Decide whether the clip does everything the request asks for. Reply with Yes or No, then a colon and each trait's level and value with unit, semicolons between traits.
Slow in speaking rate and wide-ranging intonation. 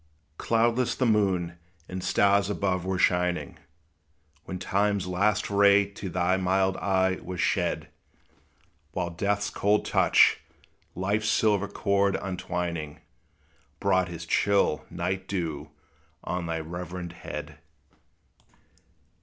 No: slow, 110 wpm; narrow, 2.4 semitones